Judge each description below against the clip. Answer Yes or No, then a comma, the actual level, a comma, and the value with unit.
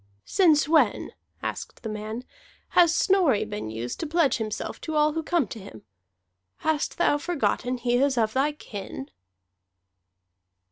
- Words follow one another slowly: No, average, 145 wpm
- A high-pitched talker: Yes, very high, 275 Hz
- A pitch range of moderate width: No, wide, 6.5 semitones